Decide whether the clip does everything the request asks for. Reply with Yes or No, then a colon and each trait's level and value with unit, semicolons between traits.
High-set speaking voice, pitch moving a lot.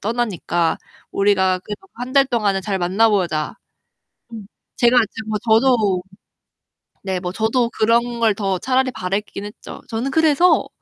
No: high, 215 Hz; average, 3.9 semitones